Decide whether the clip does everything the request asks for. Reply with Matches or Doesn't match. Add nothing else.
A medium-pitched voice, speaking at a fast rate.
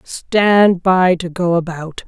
Doesn't match